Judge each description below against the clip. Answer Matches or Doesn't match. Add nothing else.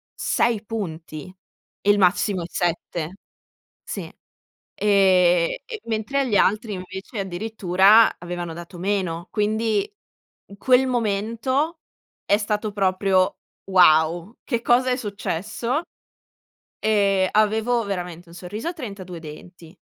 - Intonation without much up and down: Doesn't match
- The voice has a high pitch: Matches